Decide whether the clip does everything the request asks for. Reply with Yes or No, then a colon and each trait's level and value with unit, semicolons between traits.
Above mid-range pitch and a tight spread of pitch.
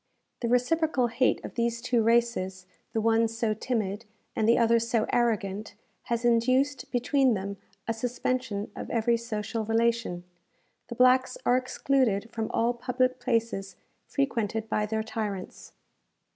Yes: high, 230 Hz; narrow, 2.2 semitones